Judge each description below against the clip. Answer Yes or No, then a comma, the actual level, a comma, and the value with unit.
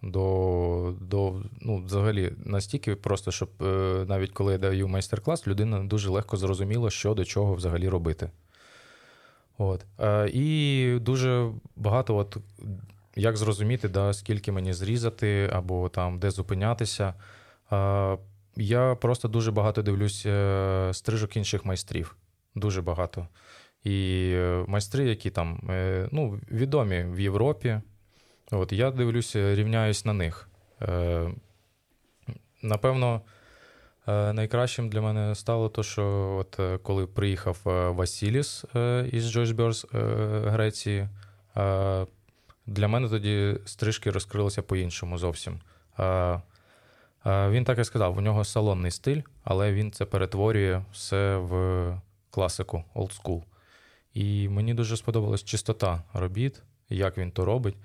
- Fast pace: No, average, 110 wpm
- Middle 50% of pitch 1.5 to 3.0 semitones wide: Yes, average, 2.7 semitones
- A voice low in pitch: Yes, low, 100 Hz